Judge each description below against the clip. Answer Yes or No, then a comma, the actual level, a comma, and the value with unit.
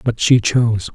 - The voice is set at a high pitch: No, low, 115 Hz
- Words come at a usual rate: Yes, average, 190 wpm